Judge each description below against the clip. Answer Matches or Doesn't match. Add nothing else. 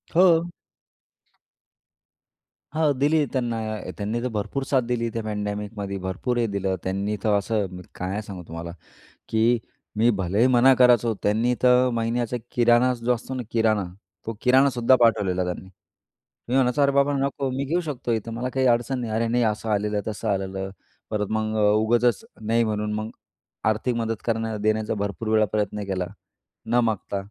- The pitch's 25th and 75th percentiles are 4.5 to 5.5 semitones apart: Doesn't match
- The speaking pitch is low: Matches